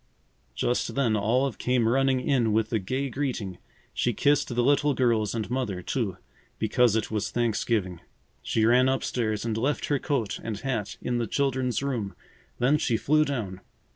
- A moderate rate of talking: Yes, average, 170 wpm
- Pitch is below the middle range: Yes, low, 120 Hz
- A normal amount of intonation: Yes, average, 3.5 semitones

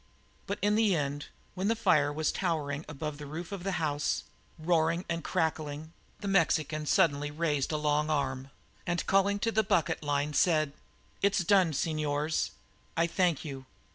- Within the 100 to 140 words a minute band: No, average, 165 wpm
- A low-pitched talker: No, medium, 155 Hz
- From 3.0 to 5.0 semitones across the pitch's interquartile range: Yes, average, 3.4 semitones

